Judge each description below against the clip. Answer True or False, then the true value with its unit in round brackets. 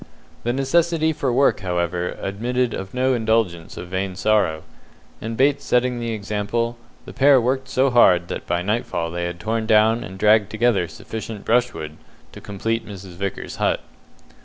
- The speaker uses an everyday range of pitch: True (4.6 semitones)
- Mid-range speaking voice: False (110 Hz)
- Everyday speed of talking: True (160 wpm)